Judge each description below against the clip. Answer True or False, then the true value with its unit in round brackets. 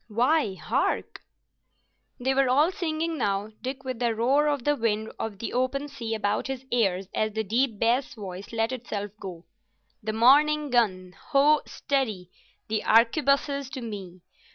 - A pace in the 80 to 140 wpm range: False (155 wpm)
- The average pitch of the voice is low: False (235 Hz)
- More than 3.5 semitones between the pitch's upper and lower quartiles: True (4.6 semitones)